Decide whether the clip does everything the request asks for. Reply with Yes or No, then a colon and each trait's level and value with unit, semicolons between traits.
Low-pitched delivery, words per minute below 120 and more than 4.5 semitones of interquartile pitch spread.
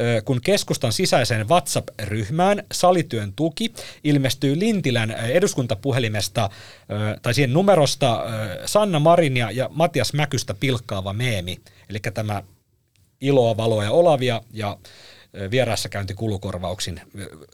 Yes: low, 120 Hz; slow, 95 wpm; average, 5.2 semitones